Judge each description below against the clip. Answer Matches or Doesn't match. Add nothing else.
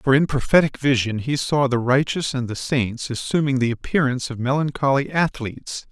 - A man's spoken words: Matches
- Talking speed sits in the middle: Matches